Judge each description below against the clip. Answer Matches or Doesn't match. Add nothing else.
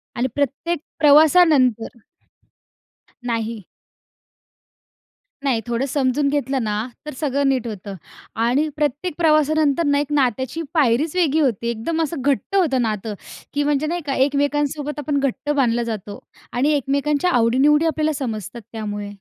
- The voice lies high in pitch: Matches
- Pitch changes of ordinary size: Matches